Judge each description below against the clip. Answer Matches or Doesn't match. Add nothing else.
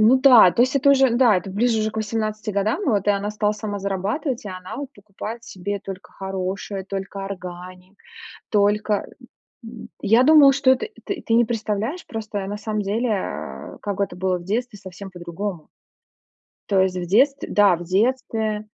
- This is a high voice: Matches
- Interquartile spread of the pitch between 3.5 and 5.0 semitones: Doesn't match